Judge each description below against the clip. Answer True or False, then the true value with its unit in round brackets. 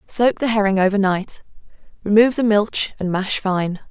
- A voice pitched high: True (205 Hz)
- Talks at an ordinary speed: True (170 wpm)